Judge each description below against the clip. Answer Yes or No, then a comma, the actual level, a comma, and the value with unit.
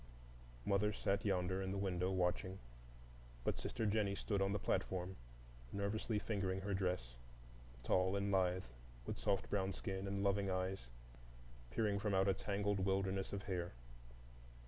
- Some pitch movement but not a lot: No, narrow, 1.3 semitones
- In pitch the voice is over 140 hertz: No, very low, 95 Hz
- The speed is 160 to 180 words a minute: No, average, 145 wpm